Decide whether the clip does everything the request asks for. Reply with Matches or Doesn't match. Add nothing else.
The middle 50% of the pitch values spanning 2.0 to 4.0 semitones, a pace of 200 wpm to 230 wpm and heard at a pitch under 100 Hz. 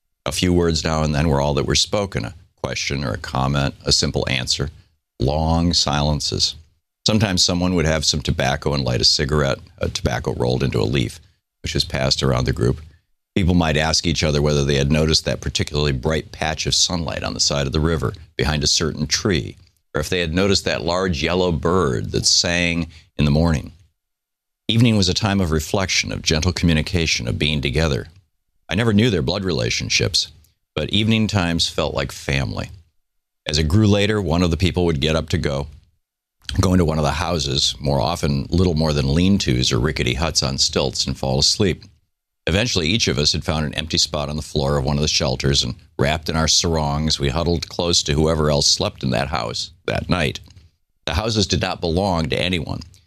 Matches